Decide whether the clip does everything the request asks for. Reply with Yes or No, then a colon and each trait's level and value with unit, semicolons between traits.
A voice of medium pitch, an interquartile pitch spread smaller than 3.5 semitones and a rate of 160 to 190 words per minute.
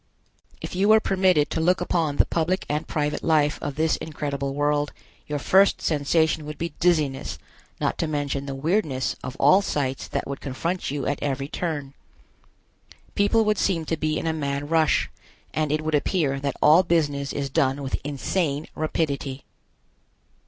Yes: medium, 150 Hz; average, 2.8 semitones; average, 170 wpm